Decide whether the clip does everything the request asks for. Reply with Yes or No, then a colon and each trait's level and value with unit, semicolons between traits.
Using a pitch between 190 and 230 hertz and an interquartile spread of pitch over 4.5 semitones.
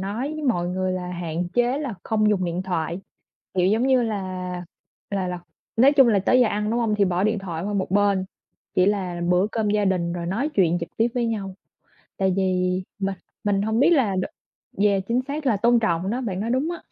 No: high, 200 Hz; average, 4.2 semitones